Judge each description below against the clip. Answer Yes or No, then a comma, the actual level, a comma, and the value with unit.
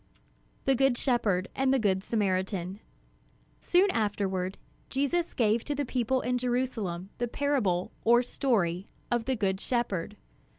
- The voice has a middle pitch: No, high, 230 Hz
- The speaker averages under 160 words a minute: Yes, slow, 135 wpm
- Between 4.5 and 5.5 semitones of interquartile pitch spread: Yes, average, 5.2 semitones